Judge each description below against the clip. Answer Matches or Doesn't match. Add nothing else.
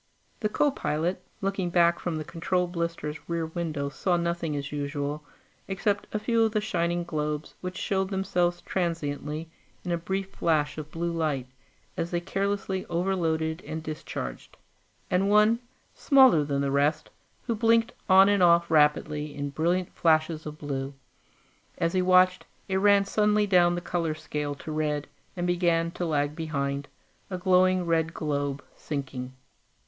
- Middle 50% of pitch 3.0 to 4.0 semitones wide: Matches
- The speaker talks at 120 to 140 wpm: Doesn't match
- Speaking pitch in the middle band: Matches